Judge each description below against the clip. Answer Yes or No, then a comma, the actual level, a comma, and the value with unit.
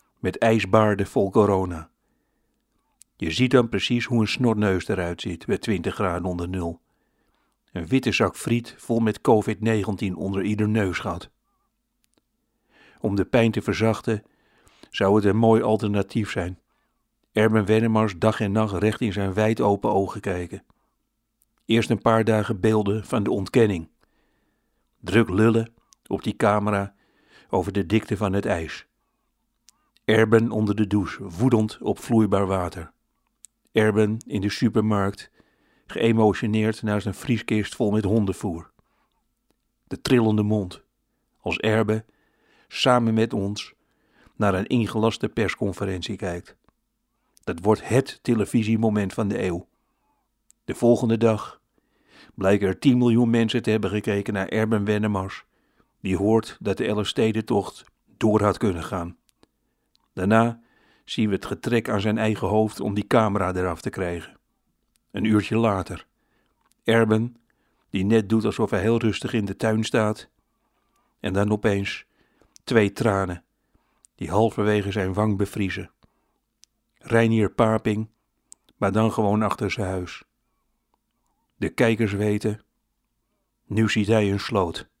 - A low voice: Yes, low, 105 Hz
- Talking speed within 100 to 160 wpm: Yes, slow, 135 wpm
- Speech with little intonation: Yes, narrow, 2.1 semitones